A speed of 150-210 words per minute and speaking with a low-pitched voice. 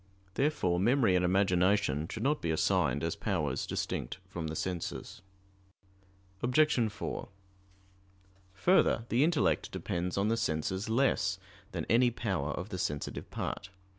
No: slow, 135 wpm; very low, 95 Hz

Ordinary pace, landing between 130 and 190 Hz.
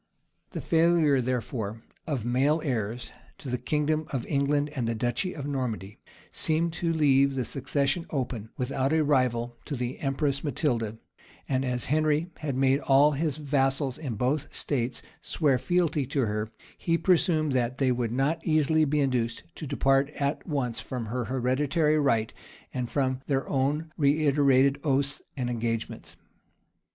Yes: average, 150 wpm; low, 135 Hz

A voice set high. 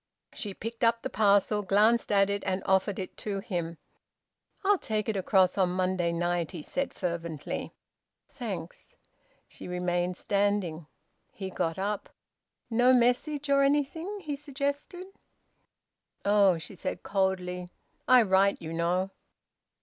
Yes: high, 195 Hz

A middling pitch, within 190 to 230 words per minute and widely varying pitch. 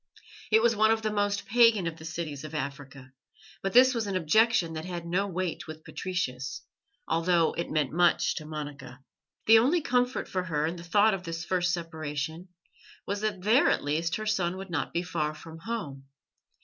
No: medium, 175 Hz; average, 195 wpm; average, 4.8 semitones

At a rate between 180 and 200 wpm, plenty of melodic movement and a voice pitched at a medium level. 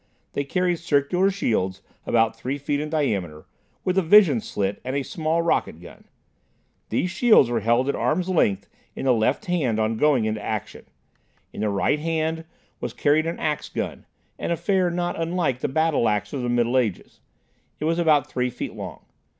Yes: average, 185 wpm; wide, 6.3 semitones; medium, 145 Hz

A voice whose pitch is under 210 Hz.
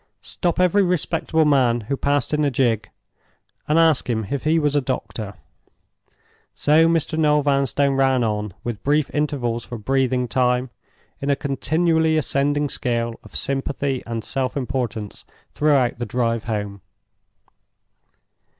Yes: low, 135 Hz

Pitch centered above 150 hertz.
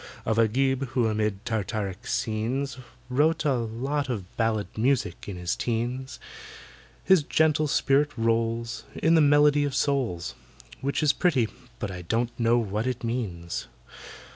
No: low, 120 Hz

